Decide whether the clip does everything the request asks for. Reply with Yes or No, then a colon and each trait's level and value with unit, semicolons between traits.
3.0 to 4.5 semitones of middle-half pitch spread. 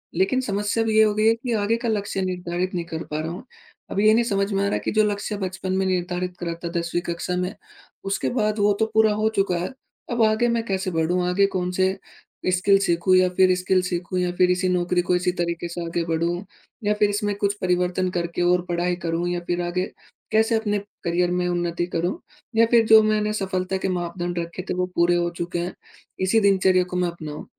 No: narrow, 2.6 semitones